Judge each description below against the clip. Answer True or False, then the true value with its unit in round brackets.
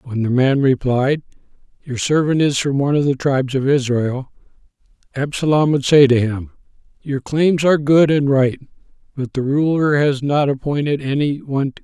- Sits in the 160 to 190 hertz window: False (140 Hz)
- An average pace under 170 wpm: False (180 wpm)